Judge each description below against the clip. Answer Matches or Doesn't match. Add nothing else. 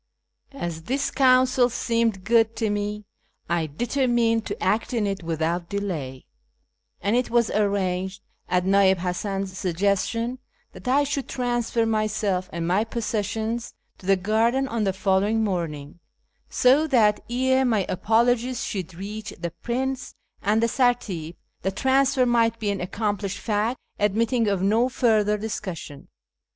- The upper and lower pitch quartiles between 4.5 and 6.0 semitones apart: Doesn't match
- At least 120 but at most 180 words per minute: Matches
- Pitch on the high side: Matches